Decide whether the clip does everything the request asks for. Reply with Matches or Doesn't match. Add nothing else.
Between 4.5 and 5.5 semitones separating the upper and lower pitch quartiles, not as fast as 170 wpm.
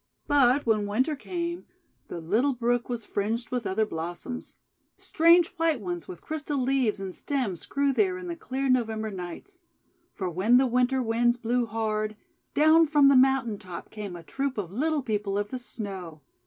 Doesn't match